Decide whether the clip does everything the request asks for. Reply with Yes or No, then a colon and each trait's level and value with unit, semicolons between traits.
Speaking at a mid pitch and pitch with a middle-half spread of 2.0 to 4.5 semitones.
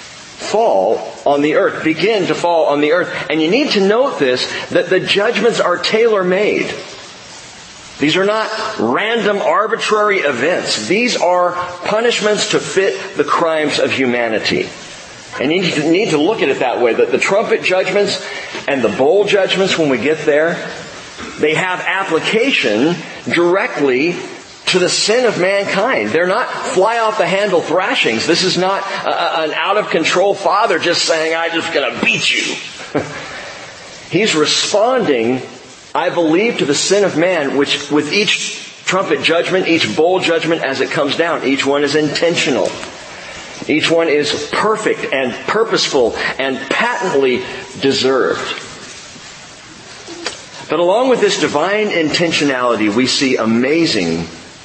No: medium, 175 Hz; wide, 5.4 semitones